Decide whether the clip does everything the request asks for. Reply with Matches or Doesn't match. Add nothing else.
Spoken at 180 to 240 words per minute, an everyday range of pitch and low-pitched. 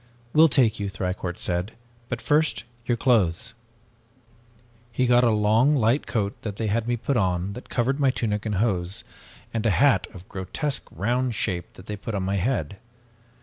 Matches